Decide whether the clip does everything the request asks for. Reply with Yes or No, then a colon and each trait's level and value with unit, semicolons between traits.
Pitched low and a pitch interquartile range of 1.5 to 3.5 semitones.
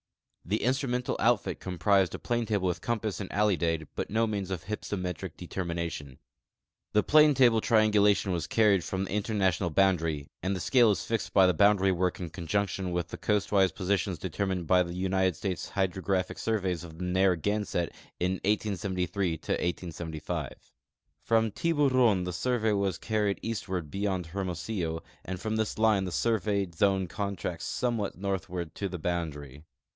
Yes: very low, 95 Hz; average, 3.1 semitones